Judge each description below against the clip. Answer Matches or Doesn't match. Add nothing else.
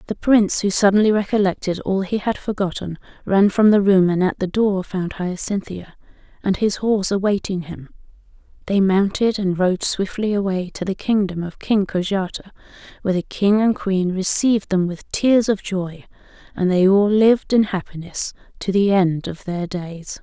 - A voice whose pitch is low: Doesn't match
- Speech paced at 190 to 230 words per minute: Doesn't match